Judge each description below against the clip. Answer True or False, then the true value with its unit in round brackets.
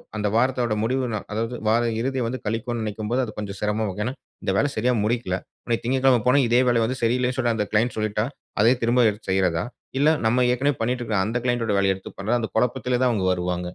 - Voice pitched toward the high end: False (115 Hz)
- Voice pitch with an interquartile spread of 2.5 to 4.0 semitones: True (2.9 semitones)